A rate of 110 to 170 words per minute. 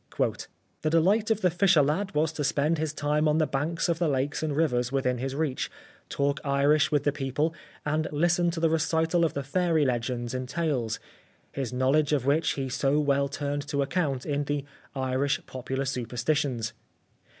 No: average, 190 wpm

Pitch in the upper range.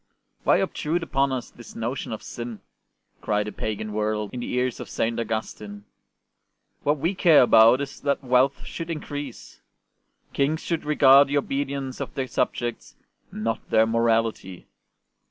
No: low, 125 Hz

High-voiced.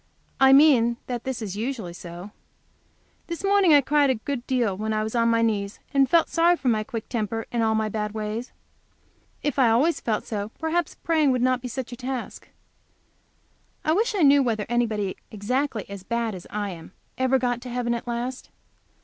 Yes: high, 240 Hz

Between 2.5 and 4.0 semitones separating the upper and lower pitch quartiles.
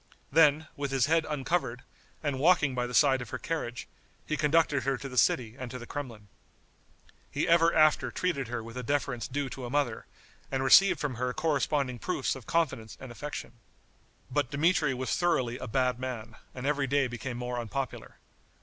Yes: average, 3.2 semitones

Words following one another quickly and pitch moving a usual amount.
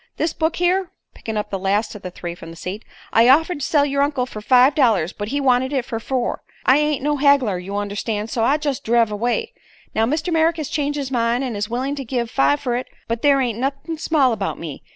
Yes: fast, 245 wpm; average, 4.8 semitones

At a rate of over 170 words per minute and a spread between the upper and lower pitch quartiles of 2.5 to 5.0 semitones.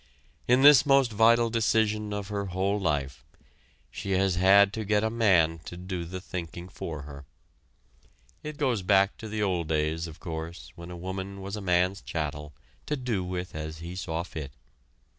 Yes: average, 180 wpm; average, 4.0 semitones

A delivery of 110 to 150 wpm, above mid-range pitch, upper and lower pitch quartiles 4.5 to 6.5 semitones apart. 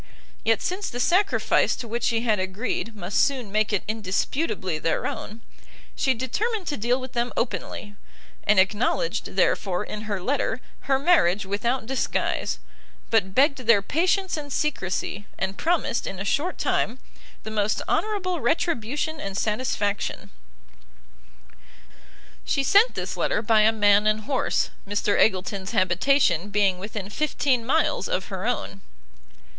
Yes: average, 140 wpm; high, 225 Hz; wide, 5.5 semitones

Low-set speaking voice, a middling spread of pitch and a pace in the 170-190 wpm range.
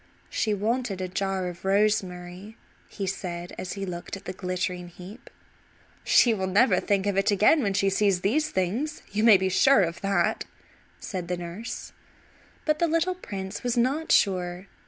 No: high, 195 Hz; average, 3.4 semitones; average, 175 wpm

